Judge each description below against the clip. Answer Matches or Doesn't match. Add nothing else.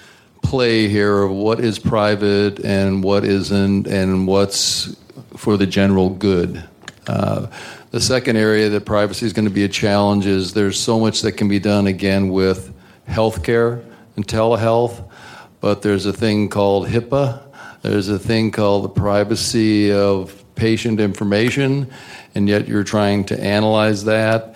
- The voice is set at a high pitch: Doesn't match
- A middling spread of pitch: Doesn't match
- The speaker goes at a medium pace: Matches